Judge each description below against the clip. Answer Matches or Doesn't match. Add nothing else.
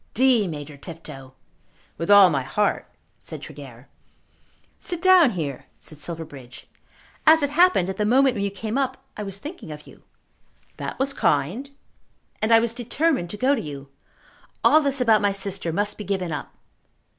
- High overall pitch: Matches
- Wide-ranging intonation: Matches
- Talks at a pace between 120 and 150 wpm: Doesn't match